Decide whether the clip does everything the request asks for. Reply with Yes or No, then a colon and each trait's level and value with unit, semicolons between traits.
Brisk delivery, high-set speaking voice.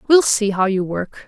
Yes: fast, 235 wpm; high, 210 Hz